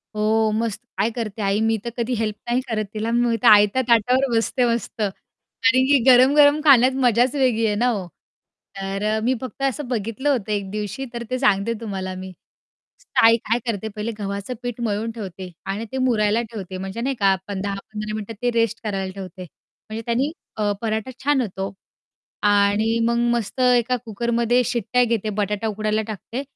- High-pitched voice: Yes, high, 225 Hz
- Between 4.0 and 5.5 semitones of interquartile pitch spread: No, average, 2.9 semitones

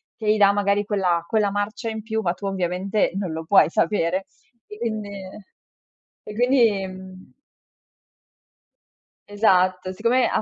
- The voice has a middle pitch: No, high, 200 Hz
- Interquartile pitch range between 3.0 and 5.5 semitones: No, narrow, 2.5 semitones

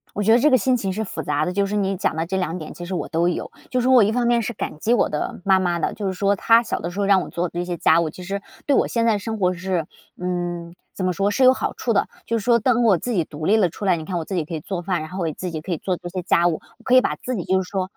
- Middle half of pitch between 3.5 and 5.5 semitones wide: Yes, average, 4.0 semitones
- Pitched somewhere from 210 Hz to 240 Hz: No, high, 190 Hz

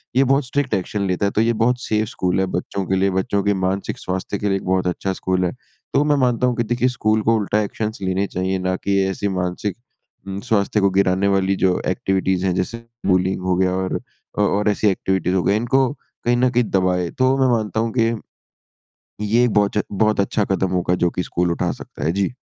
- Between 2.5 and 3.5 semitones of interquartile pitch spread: Yes, average, 3.2 semitones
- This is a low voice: Yes, low, 100 Hz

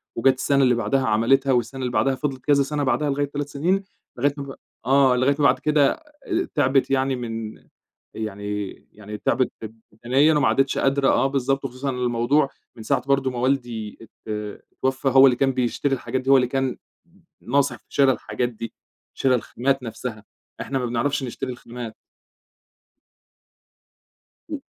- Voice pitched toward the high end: No, low, 130 Hz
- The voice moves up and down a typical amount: No, narrow, 2.3 semitones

